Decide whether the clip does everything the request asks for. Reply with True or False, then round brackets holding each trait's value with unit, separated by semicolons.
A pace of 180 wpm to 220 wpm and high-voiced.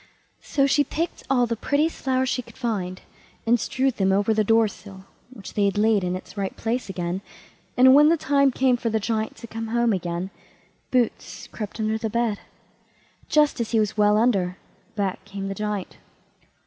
True (190 wpm; 220 Hz)